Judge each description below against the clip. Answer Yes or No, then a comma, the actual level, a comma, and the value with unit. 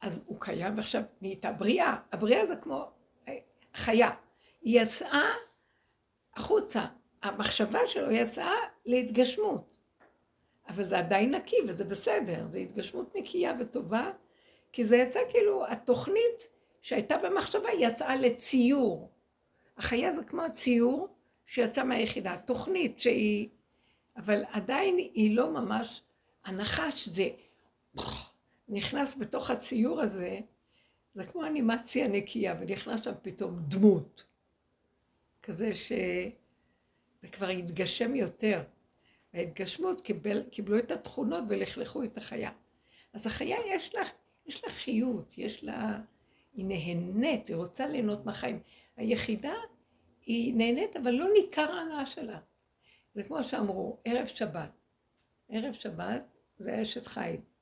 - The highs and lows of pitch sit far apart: Yes, wide, 5.8 semitones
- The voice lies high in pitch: Yes, high, 240 Hz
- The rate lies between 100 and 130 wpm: Yes, average, 115 wpm